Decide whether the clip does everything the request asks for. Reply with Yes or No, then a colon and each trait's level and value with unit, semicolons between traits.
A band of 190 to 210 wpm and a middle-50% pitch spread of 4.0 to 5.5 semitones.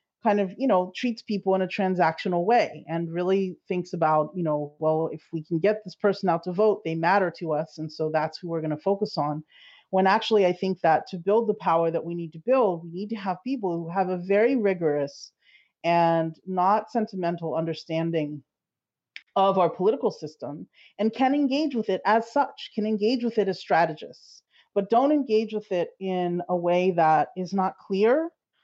Yes: average, 200 wpm; average, 4.3 semitones